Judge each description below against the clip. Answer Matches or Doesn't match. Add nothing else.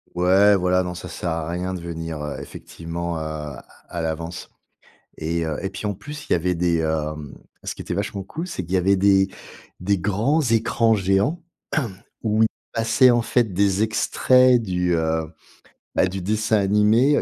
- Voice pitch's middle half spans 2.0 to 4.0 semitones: Doesn't match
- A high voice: Doesn't match